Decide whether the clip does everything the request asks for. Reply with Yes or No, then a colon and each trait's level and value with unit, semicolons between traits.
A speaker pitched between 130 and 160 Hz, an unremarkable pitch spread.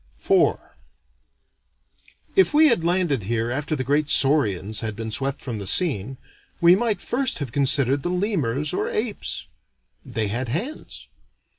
No: medium, 140 Hz; wide, 7.7 semitones